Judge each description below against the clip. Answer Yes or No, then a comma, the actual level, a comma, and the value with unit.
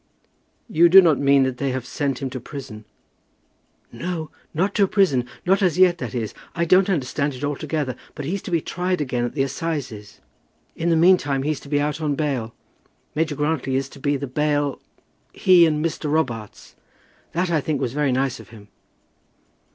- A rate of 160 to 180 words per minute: No, average, 190 wpm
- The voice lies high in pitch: No, medium, 145 Hz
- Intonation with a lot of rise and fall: No, average, 3.8 semitones